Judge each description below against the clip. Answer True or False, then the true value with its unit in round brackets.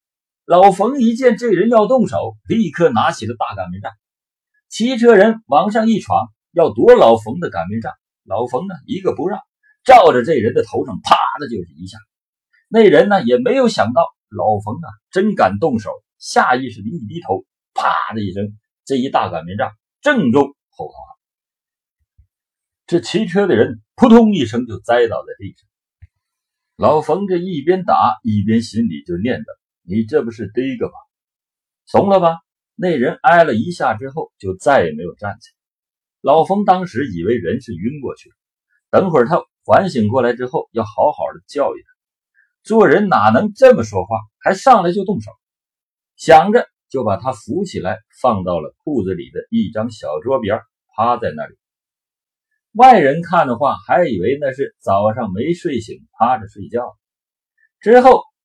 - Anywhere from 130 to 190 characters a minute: False (240 characters per minute)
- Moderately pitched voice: True (180 Hz)